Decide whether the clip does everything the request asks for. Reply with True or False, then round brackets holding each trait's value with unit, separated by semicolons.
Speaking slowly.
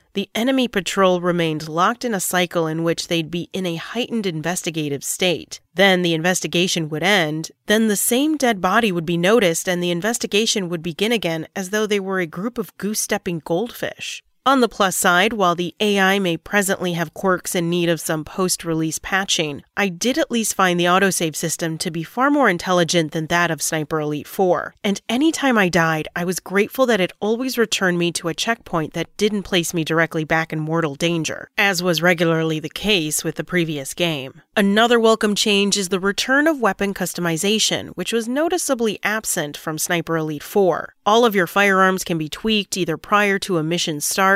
False (200 wpm)